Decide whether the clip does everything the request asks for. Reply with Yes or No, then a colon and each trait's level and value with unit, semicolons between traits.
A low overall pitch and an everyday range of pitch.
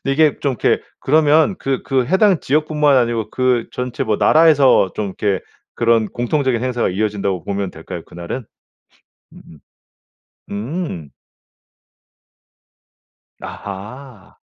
No: low, 125 Hz; wide, 6.0 semitones